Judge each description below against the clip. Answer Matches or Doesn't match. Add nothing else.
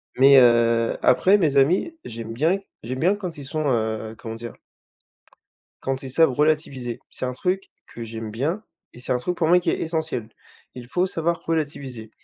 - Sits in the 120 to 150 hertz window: Matches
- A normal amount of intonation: Doesn't match